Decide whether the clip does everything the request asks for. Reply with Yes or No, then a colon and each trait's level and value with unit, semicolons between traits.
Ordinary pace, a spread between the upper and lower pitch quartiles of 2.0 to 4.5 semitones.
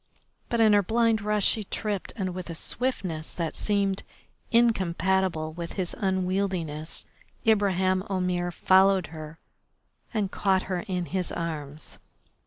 No: slow, 130 wpm; average, 2.8 semitones